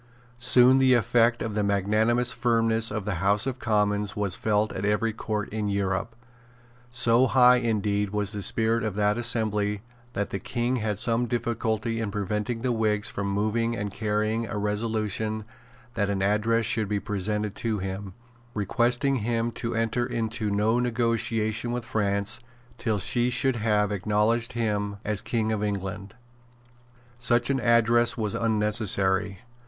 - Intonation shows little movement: Yes, narrow, 2.2 semitones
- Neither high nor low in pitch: No, low, 110 Hz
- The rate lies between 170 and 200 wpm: No, average, 155 wpm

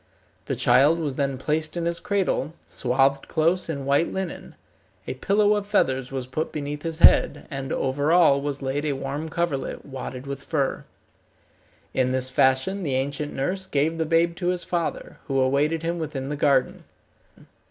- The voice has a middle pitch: Yes, medium, 145 Hz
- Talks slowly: No, average, 175 wpm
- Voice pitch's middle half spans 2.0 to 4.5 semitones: Yes, average, 3.7 semitones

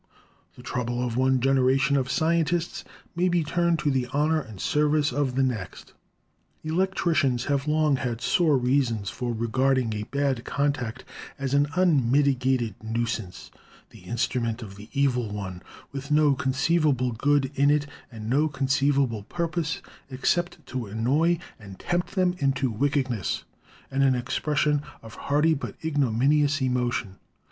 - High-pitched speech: No, low, 135 Hz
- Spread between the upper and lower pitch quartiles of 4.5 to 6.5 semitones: No, average, 3.5 semitones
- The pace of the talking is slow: No, average, 145 wpm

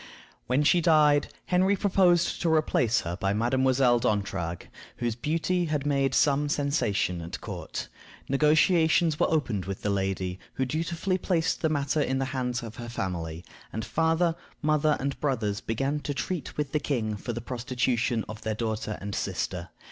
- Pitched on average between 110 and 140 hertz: Yes, low, 135 Hz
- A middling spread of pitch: No, wide, 5.8 semitones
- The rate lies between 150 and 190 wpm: Yes, average, 165 wpm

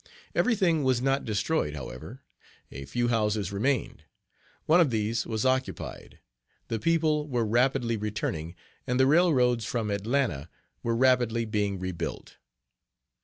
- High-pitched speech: No, low, 115 Hz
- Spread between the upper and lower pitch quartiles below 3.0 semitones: No, average, 4.3 semitones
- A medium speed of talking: No, slow, 130 wpm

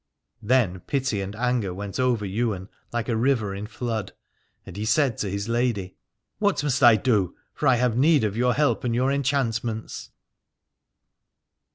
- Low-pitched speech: Yes, low, 115 Hz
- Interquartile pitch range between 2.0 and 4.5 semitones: Yes, average, 3.8 semitones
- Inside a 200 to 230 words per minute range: No, average, 165 wpm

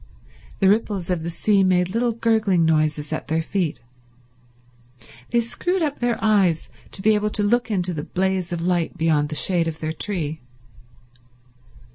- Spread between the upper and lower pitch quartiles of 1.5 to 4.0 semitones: No, average, 4.7 semitones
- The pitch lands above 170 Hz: Yes, medium, 185 Hz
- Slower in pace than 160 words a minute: No, average, 165 wpm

